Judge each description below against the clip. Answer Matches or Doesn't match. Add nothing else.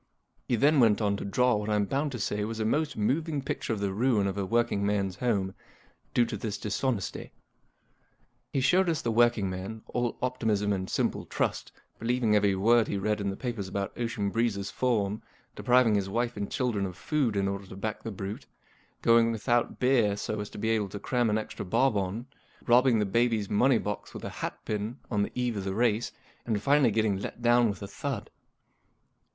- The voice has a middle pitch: Doesn't match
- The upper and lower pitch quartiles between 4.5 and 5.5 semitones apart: Doesn't match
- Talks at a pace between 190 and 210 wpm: Matches